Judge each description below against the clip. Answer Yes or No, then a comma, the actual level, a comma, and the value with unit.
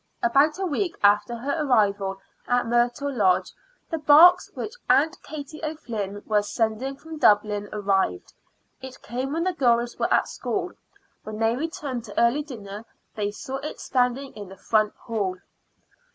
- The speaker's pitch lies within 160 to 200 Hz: No, high, 240 Hz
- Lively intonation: Yes, wide, 5.7 semitones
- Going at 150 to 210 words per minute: Yes, average, 155 wpm